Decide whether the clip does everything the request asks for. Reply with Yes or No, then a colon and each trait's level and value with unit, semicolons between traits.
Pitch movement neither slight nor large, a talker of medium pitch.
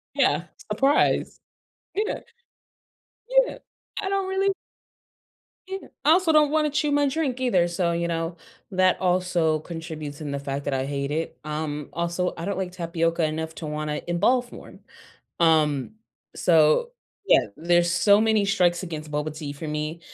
No: wide, 5.9 semitones; medium, 170 Hz